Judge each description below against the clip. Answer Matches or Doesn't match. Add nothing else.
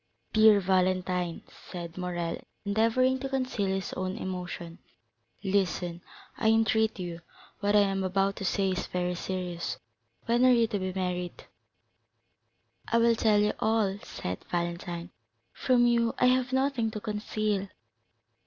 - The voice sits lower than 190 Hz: Doesn't match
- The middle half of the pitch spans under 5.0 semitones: Matches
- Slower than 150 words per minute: Matches